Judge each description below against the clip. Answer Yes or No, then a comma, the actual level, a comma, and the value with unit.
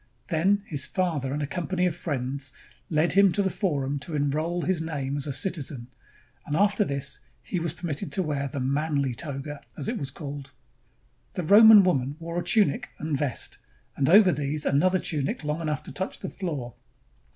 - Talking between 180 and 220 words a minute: Yes, average, 185 wpm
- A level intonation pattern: No, average, 4.4 semitones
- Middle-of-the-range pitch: Yes, medium, 155 Hz